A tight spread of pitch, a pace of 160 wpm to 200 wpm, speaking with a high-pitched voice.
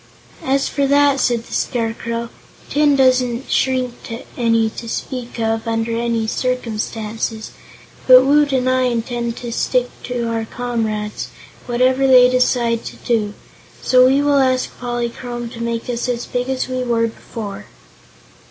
No: narrow, 1.9 semitones; average, 145 wpm; high, 240 Hz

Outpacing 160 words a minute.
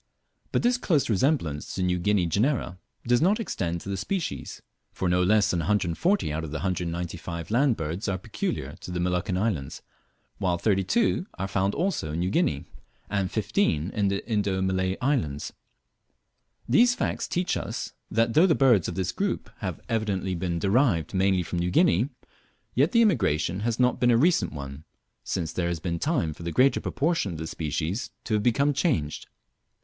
Yes: average, 180 wpm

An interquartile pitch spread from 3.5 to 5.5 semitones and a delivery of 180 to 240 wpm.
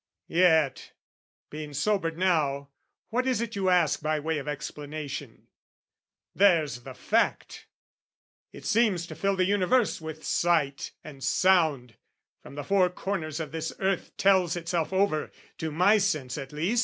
No: average, 4.3 semitones; average, 145 wpm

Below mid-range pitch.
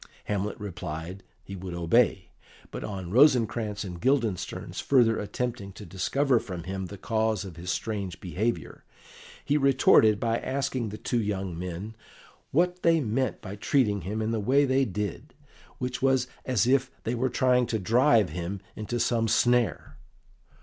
Yes: low, 110 Hz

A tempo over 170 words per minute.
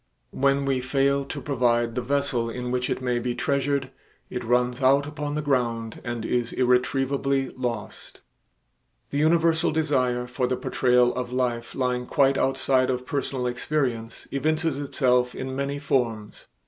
No: average, 150 wpm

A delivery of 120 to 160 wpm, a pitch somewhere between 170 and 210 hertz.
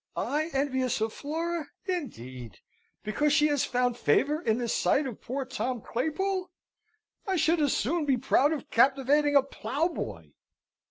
No: average, 150 wpm; very high, 280 Hz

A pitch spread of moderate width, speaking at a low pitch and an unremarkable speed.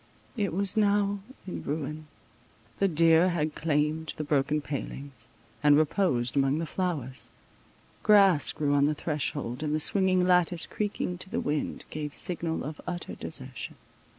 No: average, 3.8 semitones; medium, 155 Hz; average, 150 wpm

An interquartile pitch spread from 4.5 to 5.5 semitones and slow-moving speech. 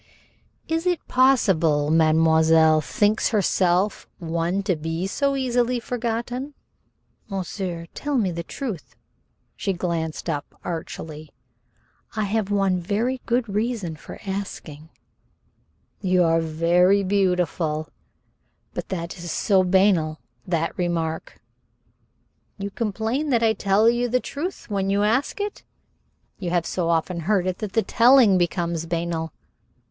Yes: average, 5.1 semitones; slow, 125 wpm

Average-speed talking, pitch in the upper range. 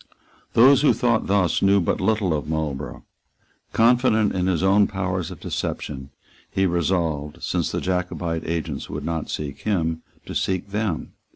No: average, 155 wpm; very low, 90 Hz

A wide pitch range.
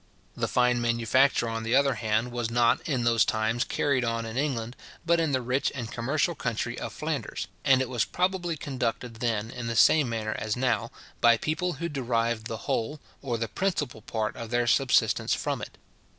No: average, 3.1 semitones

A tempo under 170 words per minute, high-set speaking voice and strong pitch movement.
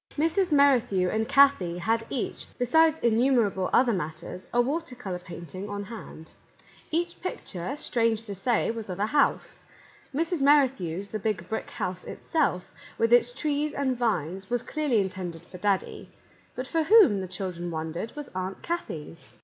Yes: average, 160 wpm; high, 225 Hz; wide, 7.1 semitones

